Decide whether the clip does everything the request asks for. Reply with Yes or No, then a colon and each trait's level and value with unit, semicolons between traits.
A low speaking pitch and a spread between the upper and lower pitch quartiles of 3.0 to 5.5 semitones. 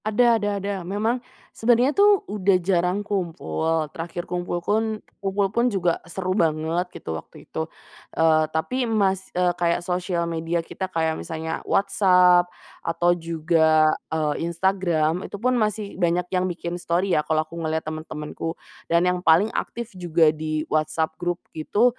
No: medium, 175 Hz; average, 3.6 semitones